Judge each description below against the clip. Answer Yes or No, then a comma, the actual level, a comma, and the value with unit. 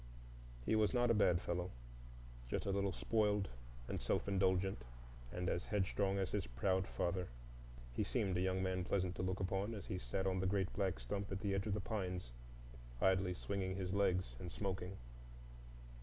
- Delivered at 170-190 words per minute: Yes, average, 180 wpm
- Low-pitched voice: Yes, very low, 95 Hz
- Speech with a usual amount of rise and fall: No, narrow, 1.7 semitones